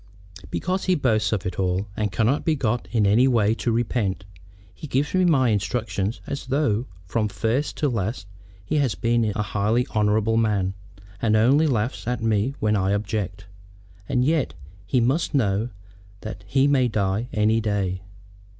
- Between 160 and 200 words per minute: Yes, average, 170 wpm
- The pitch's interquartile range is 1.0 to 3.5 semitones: No, average, 3.9 semitones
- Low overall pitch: Yes, low, 110 Hz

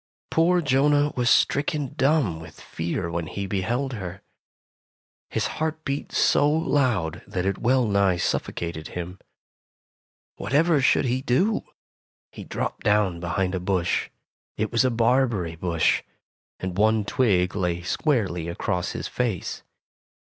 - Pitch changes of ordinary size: No, wide, 7.1 semitones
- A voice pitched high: No, low, 105 Hz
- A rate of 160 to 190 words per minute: No, slow, 135 wpm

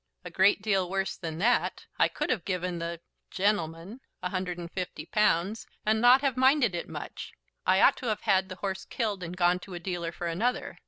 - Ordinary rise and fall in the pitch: Yes, average, 3.6 semitones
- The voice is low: No, high, 190 Hz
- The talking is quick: Yes, fast, 210 wpm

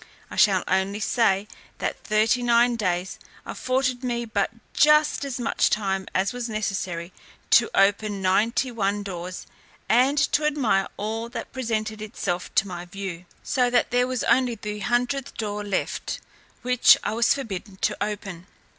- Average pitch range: Yes, average, 4.0 semitones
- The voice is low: No, high, 215 Hz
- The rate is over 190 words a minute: No, average, 155 wpm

